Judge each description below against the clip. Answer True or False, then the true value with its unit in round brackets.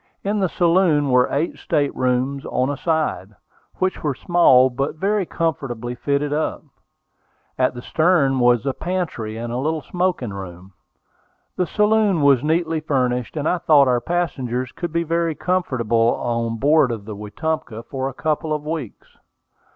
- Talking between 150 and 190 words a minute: True (160 wpm)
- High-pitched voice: False (140 Hz)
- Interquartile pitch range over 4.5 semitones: True (5.2 semitones)